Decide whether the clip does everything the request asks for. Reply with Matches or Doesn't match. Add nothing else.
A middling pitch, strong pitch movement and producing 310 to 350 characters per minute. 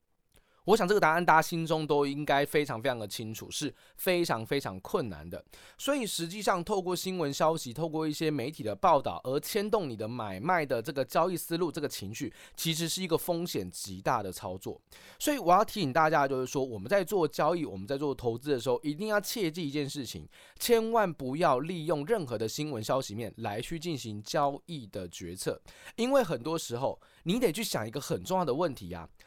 Matches